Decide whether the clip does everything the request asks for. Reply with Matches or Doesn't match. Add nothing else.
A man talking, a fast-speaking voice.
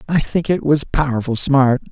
Doesn't match